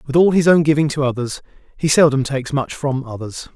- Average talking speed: No, fast, 220 wpm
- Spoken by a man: Yes, male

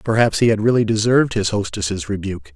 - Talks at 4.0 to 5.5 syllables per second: No, 6.1 syllables/s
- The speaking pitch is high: No, low, 105 Hz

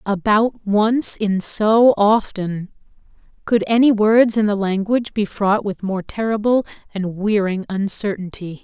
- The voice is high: Yes, high, 205 Hz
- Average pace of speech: No, slow, 130 wpm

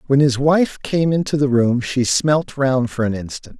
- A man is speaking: Yes, male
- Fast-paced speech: Yes, fast, 215 wpm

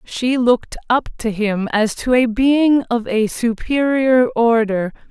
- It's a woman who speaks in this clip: Yes, female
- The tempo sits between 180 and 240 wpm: No, average, 155 wpm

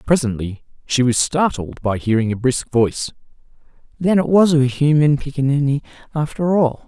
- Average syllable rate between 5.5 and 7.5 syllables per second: No, 5.1 syllables/s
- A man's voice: Yes, male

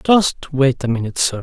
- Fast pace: Yes, fast, 210 wpm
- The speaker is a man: Yes, male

